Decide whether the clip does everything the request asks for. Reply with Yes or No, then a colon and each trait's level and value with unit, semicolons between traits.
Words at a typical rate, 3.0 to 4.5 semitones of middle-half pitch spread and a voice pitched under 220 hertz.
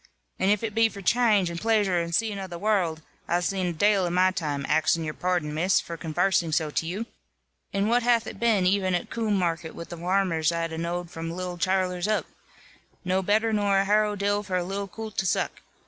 No: fast, 225 wpm; average, 3.3 semitones; medium, 185 Hz